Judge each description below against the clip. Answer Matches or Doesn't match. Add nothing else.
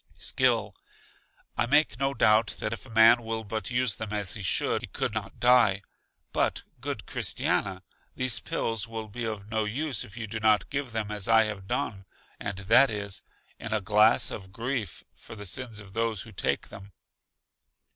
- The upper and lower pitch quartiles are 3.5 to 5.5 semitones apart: Doesn't match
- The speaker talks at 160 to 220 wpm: Matches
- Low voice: Matches